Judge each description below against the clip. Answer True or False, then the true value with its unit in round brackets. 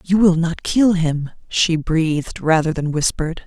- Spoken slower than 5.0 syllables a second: True (4.4 syllables/s)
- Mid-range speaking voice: True (165 Hz)